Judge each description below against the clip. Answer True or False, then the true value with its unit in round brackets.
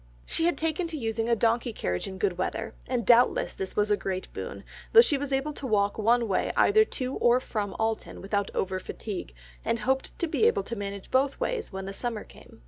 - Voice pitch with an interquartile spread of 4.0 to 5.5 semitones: True (5.2 semitones)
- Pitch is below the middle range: False (230 Hz)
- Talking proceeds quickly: True (220 wpm)